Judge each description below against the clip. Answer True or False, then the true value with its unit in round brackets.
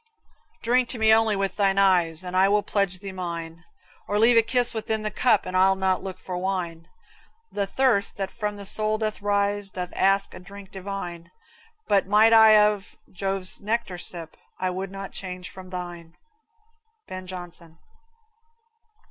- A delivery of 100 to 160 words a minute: False (170 wpm)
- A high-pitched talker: True (195 Hz)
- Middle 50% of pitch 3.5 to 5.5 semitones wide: False (2.4 semitones)